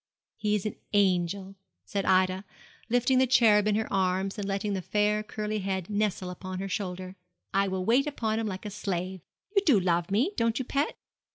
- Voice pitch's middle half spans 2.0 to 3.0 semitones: Yes, narrow, 2.5 semitones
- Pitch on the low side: No, high, 200 Hz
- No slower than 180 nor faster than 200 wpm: Yes, average, 195 wpm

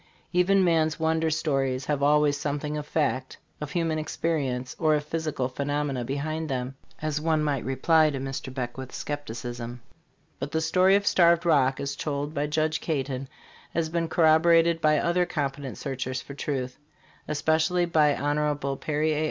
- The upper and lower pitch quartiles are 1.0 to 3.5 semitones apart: Yes, average, 2.8 semitones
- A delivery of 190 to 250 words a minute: No, average, 160 wpm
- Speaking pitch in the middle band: Yes, medium, 150 Hz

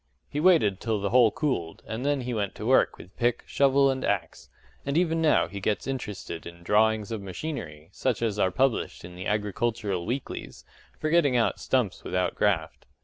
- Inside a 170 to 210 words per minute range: Yes, average, 190 wpm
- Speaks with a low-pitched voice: Yes, low, 110 Hz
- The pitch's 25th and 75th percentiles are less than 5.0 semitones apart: No, wide, 5.5 semitones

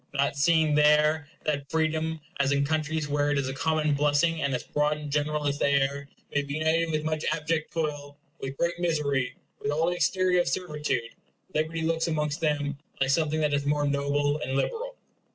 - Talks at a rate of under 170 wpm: No, average, 195 wpm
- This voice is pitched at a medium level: Yes, medium, 150 Hz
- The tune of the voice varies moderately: No, narrow, 1.9 semitones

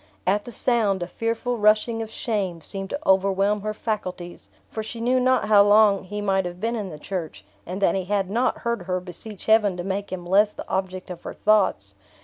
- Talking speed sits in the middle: No, fast, 215 wpm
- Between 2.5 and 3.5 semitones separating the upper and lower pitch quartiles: Yes, average, 2.8 semitones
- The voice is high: Yes, high, 200 Hz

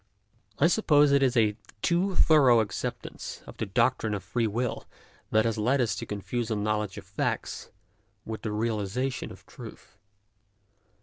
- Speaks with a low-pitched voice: Yes, low, 115 Hz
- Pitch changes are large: No, average, 4.0 semitones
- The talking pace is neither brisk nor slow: Yes, average, 160 wpm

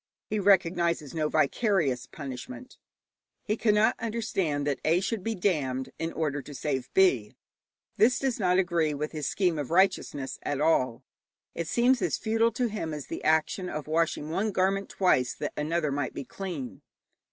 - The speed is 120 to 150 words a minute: No, average, 165 wpm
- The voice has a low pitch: No, medium, 165 Hz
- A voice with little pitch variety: No, average, 5.3 semitones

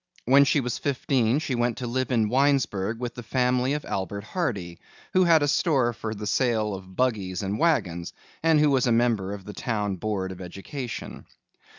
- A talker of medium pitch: No, low, 120 Hz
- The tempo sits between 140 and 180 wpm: No, average, 195 wpm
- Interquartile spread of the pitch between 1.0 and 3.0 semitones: No, average, 4.8 semitones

